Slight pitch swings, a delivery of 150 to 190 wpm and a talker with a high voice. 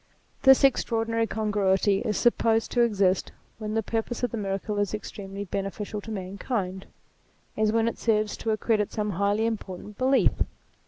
Yes: narrow, 2.2 semitones; average, 155 wpm; high, 215 Hz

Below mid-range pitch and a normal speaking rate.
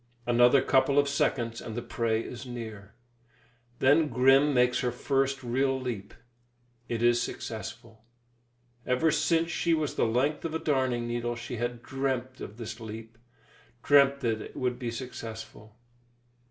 Yes: low, 125 Hz; average, 150 wpm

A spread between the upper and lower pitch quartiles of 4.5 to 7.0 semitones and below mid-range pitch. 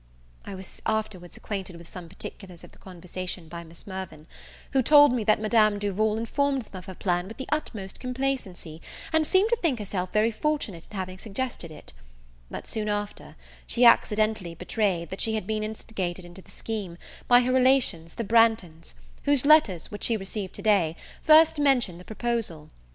No: average, 4.8 semitones; high, 210 Hz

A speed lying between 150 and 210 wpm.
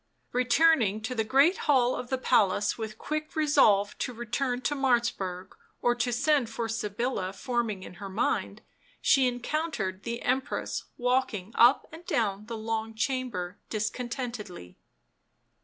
No: average, 140 wpm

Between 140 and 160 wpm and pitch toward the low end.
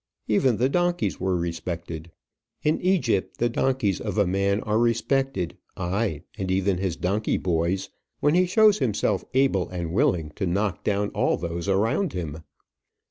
Yes: average, 155 wpm; low, 100 Hz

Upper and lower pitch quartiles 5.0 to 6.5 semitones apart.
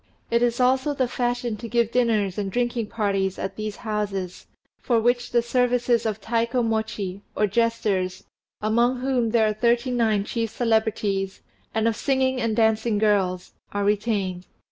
No: average, 2.7 semitones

